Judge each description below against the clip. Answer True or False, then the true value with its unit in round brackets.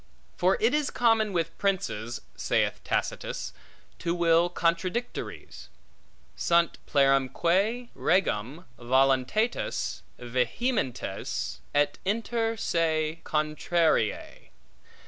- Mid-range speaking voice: True (170 Hz)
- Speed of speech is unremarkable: False (80 wpm)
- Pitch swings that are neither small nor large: False (7.6 semitones)